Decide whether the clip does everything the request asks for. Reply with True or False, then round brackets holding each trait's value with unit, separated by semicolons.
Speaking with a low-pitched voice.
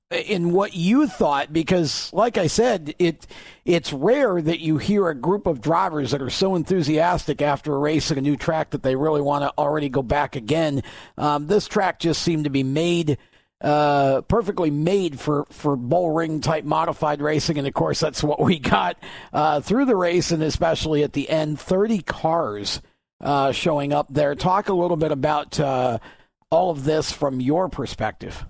False (155 Hz)